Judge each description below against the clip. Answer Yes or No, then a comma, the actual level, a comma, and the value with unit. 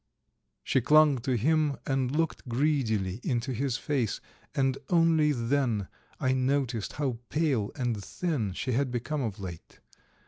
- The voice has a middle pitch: No, low, 130 Hz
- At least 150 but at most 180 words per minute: No, average, 140 wpm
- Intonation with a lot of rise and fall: No, average, 4.1 semitones